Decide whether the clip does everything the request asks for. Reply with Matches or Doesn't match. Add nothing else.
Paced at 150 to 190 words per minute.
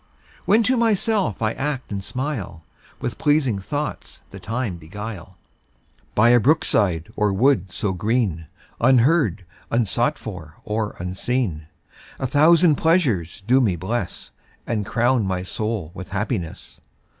Doesn't match